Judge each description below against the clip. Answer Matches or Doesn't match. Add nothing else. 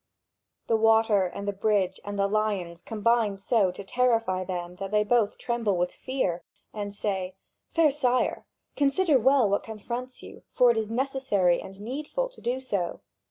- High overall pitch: Matches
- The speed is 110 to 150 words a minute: Doesn't match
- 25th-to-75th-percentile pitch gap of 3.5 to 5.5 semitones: Matches